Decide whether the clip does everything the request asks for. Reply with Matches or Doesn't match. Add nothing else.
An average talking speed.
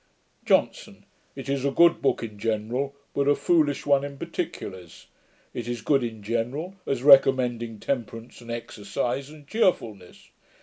Matches